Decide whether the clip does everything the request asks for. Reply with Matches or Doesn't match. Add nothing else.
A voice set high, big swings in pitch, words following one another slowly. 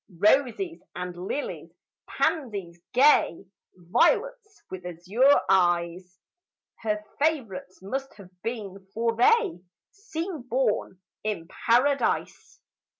Matches